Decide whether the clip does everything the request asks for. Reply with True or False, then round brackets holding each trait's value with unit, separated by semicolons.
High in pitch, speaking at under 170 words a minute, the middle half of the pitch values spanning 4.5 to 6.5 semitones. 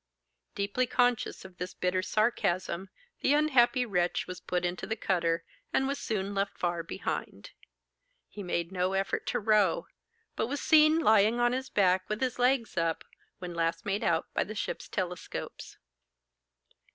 True (200 Hz; 160 wpm; 5.2 semitones)